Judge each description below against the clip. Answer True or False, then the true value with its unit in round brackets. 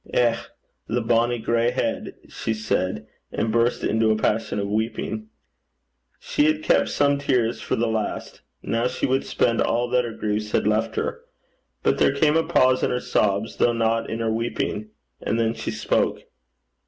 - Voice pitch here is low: True (115 Hz)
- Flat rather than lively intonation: True (1.9 semitones)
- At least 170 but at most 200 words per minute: True (180 wpm)